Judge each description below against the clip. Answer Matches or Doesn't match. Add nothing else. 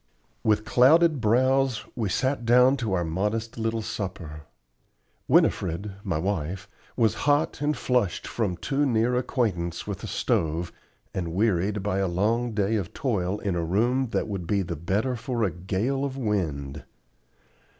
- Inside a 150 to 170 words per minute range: Matches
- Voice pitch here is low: Matches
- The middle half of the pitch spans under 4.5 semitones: Doesn't match